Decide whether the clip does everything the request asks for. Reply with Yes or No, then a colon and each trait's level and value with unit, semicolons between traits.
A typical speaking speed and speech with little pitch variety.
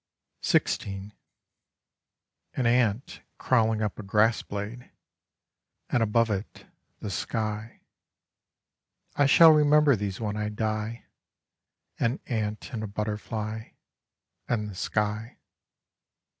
No: slow, 100 wpm; narrow, 1.9 semitones